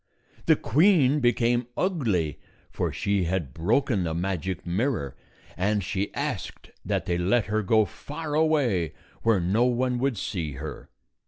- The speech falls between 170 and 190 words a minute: No, average, 145 wpm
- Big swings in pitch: Yes, wide, 6.2 semitones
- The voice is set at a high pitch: No, low, 105 Hz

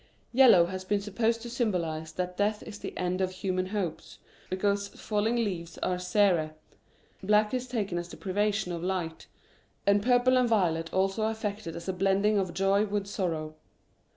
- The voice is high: Yes, high, 195 Hz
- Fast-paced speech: No, average, 165 wpm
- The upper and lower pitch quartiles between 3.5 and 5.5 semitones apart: No, average, 2.8 semitones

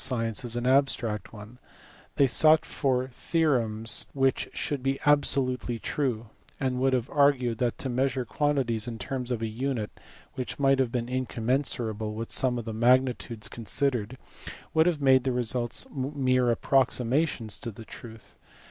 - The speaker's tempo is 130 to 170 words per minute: Yes, average, 155 wpm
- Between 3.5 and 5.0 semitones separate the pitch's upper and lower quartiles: No, average, 2.8 semitones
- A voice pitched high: No, low, 125 Hz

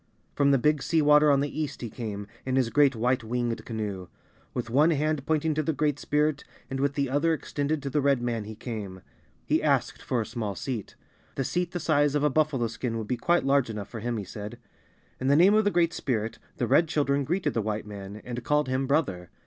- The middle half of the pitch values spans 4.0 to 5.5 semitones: Yes, average, 4.5 semitones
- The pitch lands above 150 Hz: No, low, 135 Hz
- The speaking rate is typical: No, fast, 235 wpm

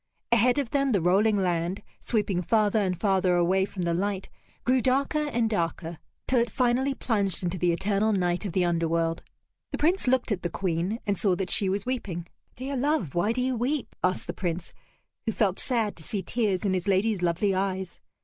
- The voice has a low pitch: No, high, 200 Hz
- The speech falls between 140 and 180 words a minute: No, average, 200 wpm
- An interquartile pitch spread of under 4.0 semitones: No, average, 4.7 semitones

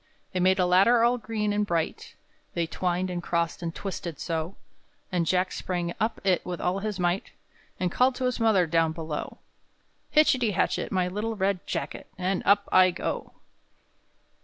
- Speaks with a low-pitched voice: No, medium, 185 Hz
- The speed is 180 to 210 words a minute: No, average, 170 wpm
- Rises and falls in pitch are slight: No, average, 3.1 semitones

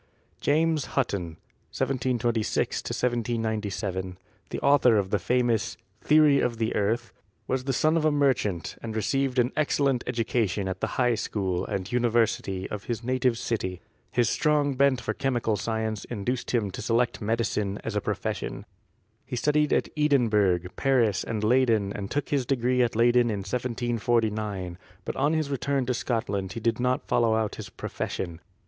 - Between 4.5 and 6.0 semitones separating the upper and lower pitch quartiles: No, average, 3.6 semitones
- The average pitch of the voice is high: No, low, 120 Hz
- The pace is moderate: Yes, average, 160 wpm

